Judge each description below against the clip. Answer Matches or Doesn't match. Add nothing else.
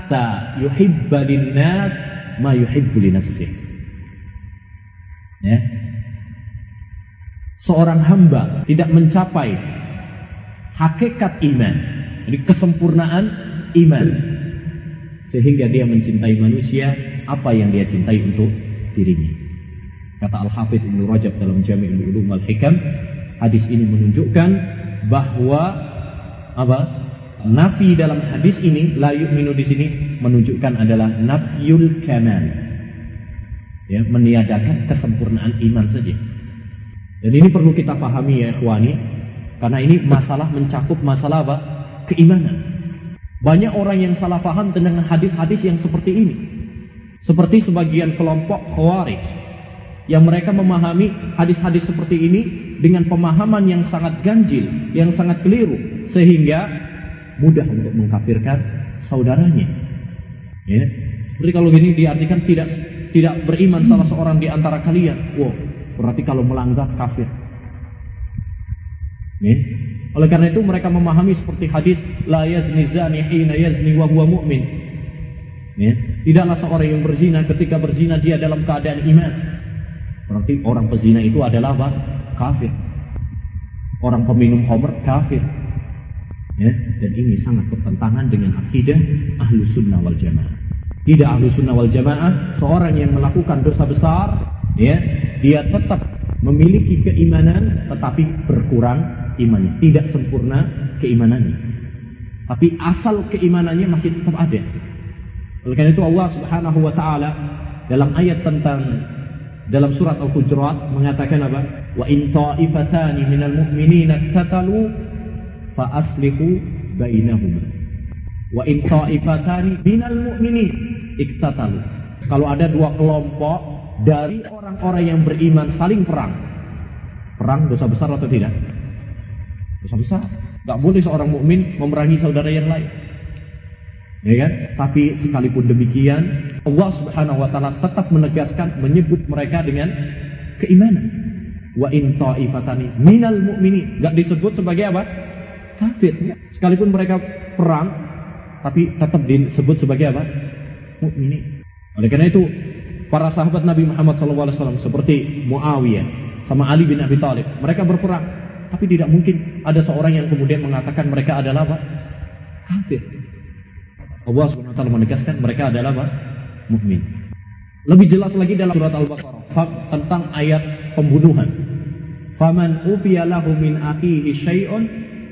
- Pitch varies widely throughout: Matches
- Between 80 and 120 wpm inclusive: Matches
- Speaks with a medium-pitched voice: Matches